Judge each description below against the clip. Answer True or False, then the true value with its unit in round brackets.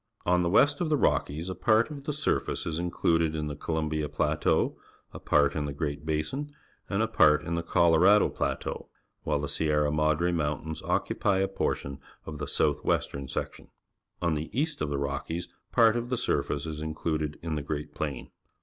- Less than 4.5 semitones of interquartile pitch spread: True (3.8 semitones)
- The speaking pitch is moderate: False (80 Hz)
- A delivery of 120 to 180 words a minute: False (190 wpm)